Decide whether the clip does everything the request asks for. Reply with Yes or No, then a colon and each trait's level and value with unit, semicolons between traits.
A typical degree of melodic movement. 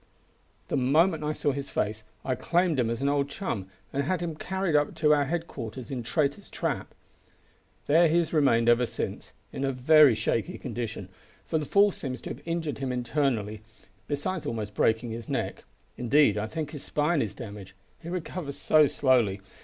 Yes: average, 5.0 semitones